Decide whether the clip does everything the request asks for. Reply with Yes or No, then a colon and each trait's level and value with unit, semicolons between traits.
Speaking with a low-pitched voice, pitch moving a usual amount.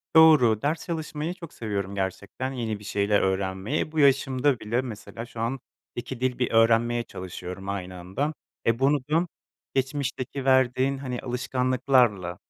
Yes: low, 125 Hz; average, 4.8 semitones